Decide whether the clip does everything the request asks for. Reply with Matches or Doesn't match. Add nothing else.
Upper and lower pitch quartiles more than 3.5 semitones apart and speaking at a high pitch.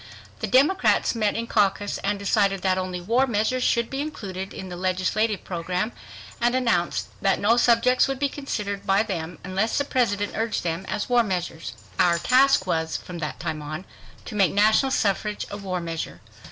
Matches